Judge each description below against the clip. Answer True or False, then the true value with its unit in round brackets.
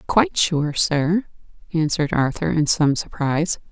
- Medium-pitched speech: True (160 Hz)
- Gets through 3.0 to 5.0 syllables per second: True (4.6 syllables/s)